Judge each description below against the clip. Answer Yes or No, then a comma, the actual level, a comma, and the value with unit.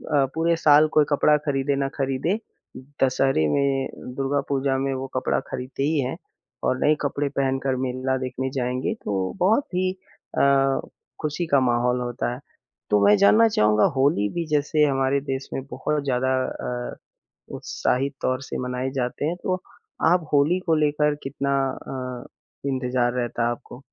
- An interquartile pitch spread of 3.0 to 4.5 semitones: No, narrow, 2.5 semitones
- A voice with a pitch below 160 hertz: Yes, low, 135 Hz